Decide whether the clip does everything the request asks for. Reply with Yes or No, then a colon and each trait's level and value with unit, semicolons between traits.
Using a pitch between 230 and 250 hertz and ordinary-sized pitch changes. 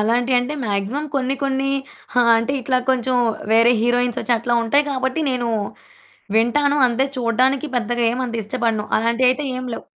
No: high, 245 Hz; narrow, 2.2 semitones